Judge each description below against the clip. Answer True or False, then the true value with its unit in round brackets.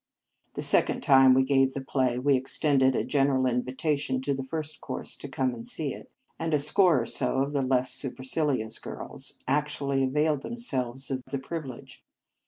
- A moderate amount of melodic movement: False (2.1 semitones)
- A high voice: False (135 Hz)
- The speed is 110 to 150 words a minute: False (185 wpm)